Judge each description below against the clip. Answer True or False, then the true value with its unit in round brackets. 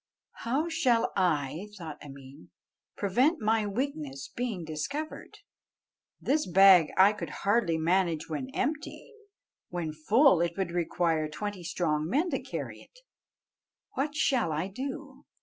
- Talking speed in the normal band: False (130 wpm)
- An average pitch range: False (8.3 semitones)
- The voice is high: True (195 Hz)